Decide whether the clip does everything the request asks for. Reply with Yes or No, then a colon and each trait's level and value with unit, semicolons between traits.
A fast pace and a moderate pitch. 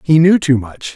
Yes: fast, 250 wpm; medium, 150 Hz